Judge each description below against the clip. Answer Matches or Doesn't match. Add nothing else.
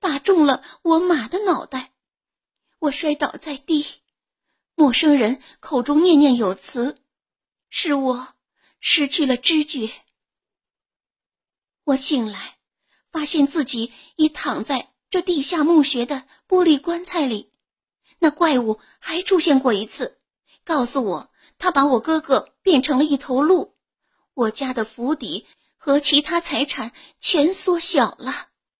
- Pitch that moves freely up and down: Doesn't match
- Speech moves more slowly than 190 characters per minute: Matches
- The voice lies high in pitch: Matches